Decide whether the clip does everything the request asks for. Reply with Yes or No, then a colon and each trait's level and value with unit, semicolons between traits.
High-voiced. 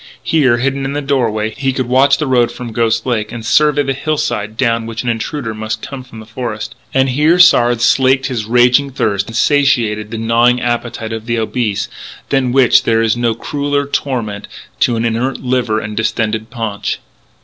No: low, 120 Hz